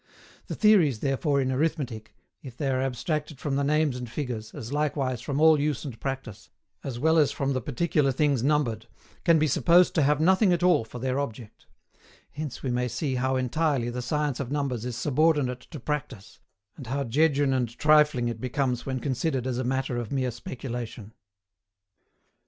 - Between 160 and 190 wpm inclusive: Yes, average, 185 wpm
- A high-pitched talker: No, low, 135 Hz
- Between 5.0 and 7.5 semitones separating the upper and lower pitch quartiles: No, average, 3.2 semitones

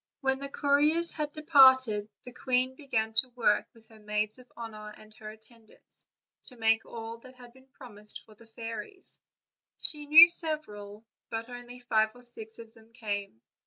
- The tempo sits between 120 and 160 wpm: No, average, 170 wpm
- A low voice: No, high, 235 Hz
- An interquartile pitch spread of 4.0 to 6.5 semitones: No, average, 3.2 semitones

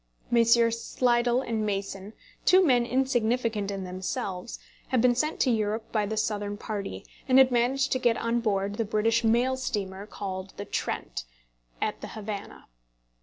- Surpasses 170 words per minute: No, average, 160 wpm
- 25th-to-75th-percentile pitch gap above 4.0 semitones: No, average, 3.1 semitones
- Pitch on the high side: Yes, high, 225 Hz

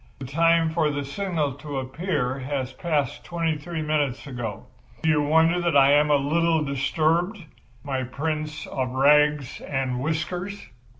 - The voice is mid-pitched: Yes, medium, 150 Hz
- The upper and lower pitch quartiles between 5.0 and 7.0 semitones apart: No, average, 3.1 semitones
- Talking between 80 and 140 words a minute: No, average, 155 wpm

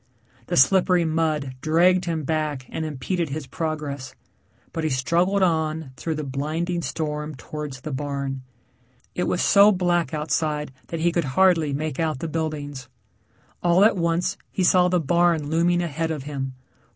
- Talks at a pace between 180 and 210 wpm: No, average, 160 wpm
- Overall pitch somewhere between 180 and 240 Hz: No, medium, 160 Hz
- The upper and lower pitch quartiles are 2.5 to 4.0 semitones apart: Yes, average, 2.9 semitones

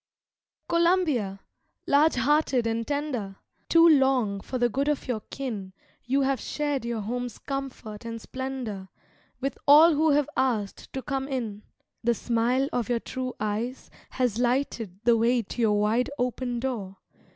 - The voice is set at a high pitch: Yes, very high, 250 Hz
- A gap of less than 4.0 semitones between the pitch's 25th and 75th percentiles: Yes, average, 3.3 semitones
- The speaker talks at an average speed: Yes, average, 150 wpm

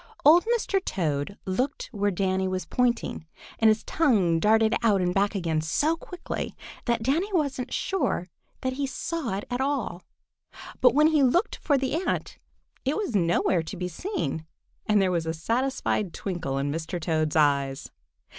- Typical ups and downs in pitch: No, wide, 8.3 semitones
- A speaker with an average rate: Yes, average, 165 wpm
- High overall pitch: Yes, high, 215 Hz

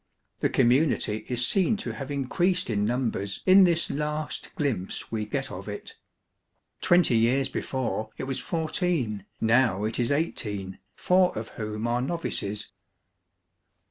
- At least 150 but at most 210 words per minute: No, average, 140 wpm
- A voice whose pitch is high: No, low, 125 Hz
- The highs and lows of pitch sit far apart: Yes, wide, 6.3 semitones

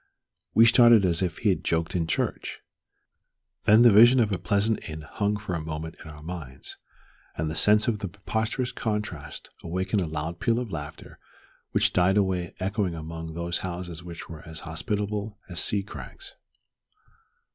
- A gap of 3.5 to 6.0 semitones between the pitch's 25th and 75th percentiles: Yes, average, 4.4 semitones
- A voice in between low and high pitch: No, very low, 90 Hz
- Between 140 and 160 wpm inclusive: No, average, 170 wpm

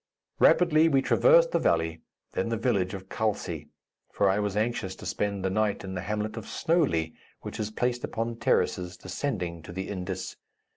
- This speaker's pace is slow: No, average, 180 wpm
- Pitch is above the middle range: No, low, 105 Hz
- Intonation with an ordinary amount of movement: Yes, average, 4.1 semitones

